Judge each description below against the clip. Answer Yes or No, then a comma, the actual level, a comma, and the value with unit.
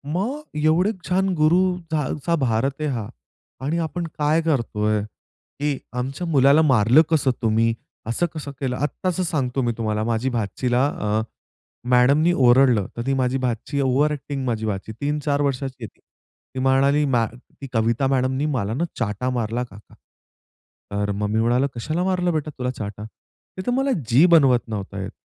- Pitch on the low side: Yes, low, 130 Hz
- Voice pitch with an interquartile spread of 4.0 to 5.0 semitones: Yes, average, 4.7 semitones